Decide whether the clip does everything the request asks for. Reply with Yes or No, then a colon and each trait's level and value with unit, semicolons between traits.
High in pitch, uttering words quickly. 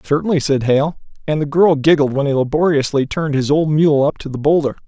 No: medium, 145 Hz; fast, 220 wpm